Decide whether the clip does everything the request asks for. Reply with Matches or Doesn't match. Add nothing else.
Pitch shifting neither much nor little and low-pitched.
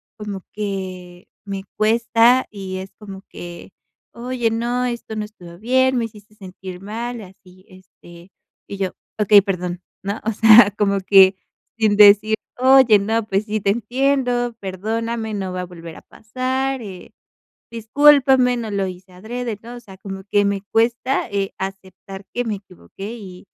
Doesn't match